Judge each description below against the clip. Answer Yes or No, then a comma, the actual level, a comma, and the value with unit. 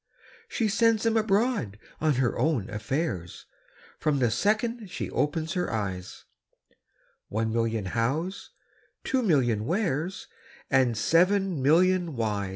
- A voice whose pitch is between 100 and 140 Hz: No, medium, 155 Hz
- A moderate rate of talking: No, slow, 120 wpm